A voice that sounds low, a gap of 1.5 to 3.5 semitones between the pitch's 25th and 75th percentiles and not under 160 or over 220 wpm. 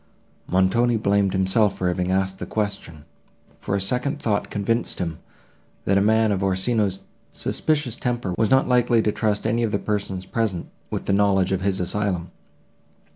Yes: low, 100 Hz; average, 3.1 semitones; average, 170 wpm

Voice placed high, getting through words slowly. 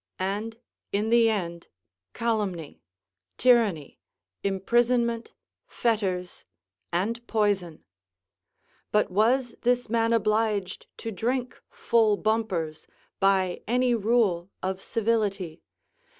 Yes: high, 215 Hz; slow, 90 wpm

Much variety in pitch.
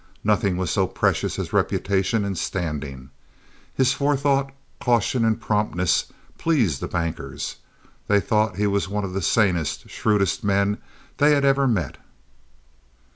No: average, 4.5 semitones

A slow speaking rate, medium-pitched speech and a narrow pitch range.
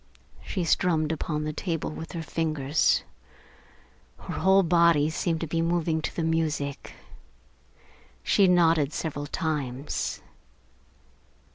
Yes: slow, 115 wpm; medium, 160 Hz; narrow, 1.8 semitones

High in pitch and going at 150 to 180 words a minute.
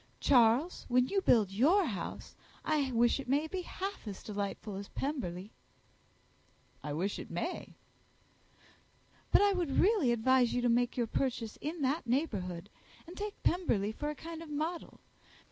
Yes: very high, 260 Hz; average, 160 wpm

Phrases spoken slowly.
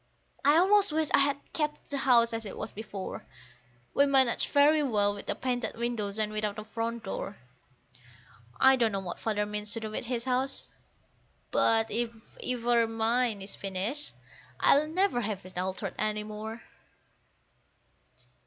No: average, 160 wpm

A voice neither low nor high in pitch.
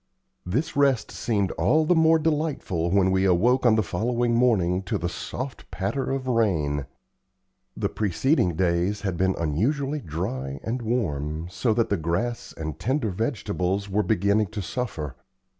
No: low, 100 Hz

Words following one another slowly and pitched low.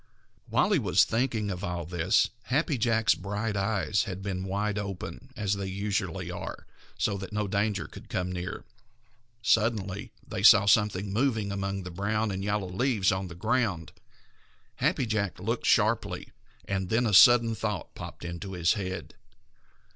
No: average, 160 wpm; low, 100 Hz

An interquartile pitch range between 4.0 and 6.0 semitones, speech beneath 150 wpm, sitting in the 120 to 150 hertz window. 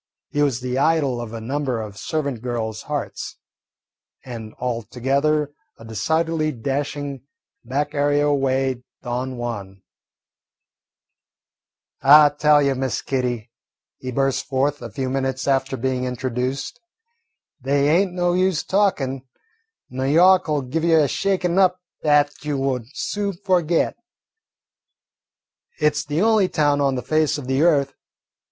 No: average, 3.2 semitones; slow, 135 wpm; medium, 140 Hz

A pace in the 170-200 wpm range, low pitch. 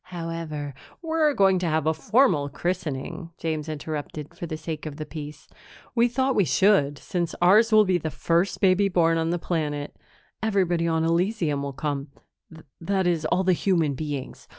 No: average, 175 wpm; medium, 165 Hz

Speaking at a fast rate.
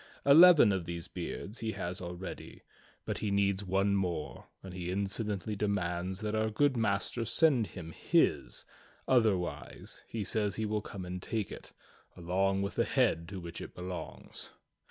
No: average, 160 wpm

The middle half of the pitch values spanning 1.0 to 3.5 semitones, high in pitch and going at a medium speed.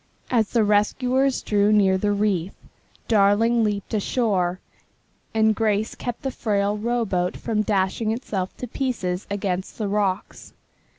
No: narrow, 2.4 semitones; high, 210 Hz; slow, 130 wpm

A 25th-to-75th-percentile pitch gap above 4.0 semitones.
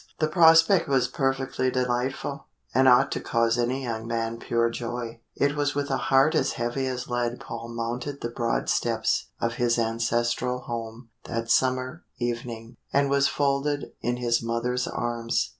No: narrow, 2.4 semitones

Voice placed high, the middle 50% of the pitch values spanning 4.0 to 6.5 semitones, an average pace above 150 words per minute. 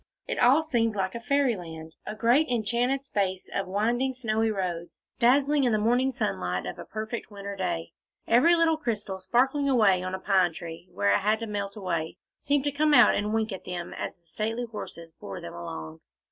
Yes: high, 215 Hz; average, 5.3 semitones; average, 195 wpm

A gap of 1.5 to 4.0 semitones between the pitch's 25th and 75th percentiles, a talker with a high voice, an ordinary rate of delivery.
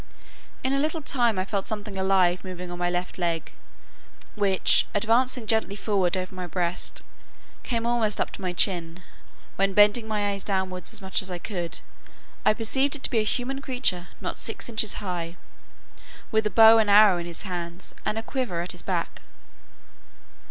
Yes: average, 3.6 semitones; high, 200 Hz; average, 180 wpm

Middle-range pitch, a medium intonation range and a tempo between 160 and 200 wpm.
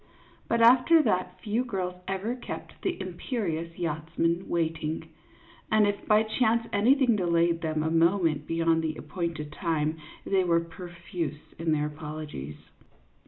No: medium, 170 Hz; average, 4.2 semitones; average, 140 wpm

